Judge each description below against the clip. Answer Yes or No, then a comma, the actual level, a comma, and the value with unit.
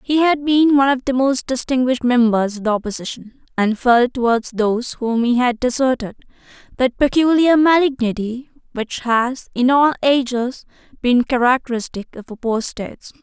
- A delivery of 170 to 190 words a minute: No, average, 145 wpm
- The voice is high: Yes, very high, 250 Hz